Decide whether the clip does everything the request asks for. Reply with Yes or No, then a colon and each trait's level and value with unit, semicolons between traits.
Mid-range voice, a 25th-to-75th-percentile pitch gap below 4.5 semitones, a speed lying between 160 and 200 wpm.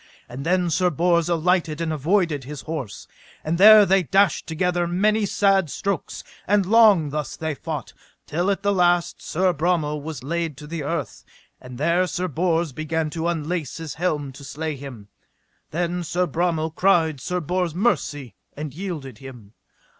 Yes: medium, 165 Hz; average, 3.2 semitones; average, 165 wpm